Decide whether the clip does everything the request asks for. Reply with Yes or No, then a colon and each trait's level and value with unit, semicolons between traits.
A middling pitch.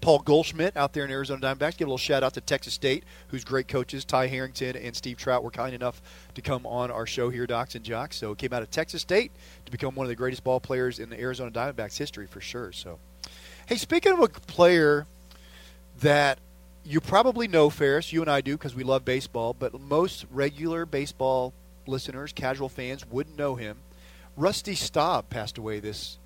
No: low, 130 Hz